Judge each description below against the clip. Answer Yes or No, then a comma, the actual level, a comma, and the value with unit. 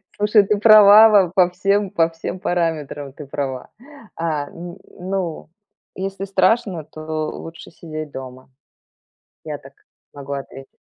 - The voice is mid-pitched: Yes, medium, 170 Hz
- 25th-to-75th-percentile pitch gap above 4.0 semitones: Yes, average, 4.6 semitones